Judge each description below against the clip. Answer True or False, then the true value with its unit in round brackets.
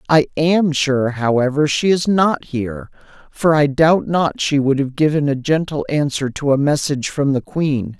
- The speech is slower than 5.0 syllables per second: True (4.5 syllables/s)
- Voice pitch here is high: False (145 Hz)